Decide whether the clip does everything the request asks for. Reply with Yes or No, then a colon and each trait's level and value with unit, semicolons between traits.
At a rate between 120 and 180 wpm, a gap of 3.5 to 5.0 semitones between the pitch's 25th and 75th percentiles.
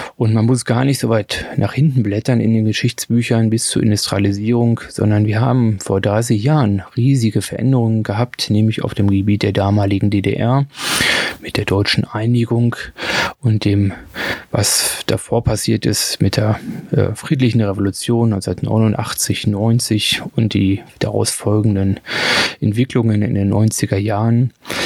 No: average, 140 wpm; average, 2.9 semitones